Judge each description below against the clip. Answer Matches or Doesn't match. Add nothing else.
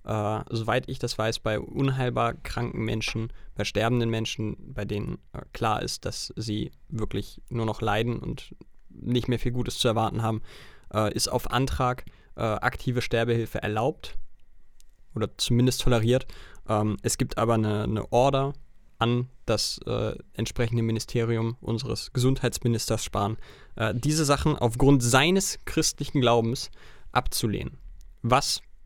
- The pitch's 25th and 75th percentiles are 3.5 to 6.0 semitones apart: Doesn't match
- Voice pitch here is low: Matches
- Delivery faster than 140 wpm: Doesn't match